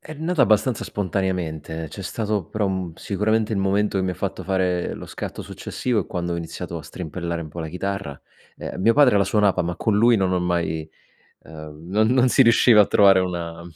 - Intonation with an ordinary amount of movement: Yes, average, 3.7 semitones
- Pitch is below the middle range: Yes, very low, 95 Hz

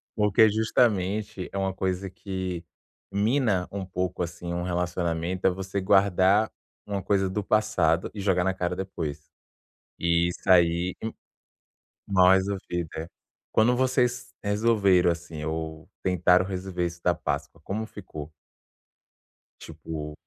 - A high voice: No, very low, 95 Hz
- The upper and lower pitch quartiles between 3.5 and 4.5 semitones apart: No, average, 2.7 semitones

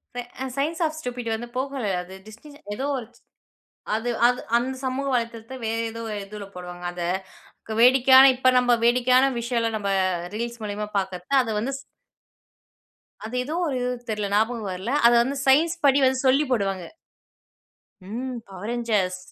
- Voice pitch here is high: Yes, high, 235 Hz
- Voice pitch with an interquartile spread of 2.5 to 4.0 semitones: Yes, average, 3.7 semitones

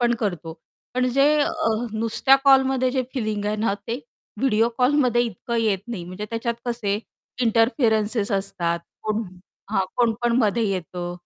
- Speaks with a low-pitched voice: No, high, 225 Hz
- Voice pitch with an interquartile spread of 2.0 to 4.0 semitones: Yes, average, 3.4 semitones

